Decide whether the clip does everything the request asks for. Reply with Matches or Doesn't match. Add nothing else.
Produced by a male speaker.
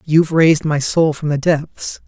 Matches